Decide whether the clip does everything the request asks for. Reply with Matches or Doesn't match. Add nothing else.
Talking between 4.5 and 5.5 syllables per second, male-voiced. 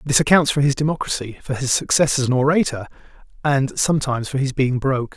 Doesn't match